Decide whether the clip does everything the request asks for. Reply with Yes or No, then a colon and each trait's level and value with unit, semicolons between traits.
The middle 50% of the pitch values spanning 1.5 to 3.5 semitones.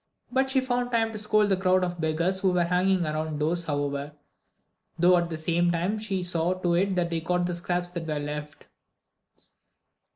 Yes: average, 2.8 semitones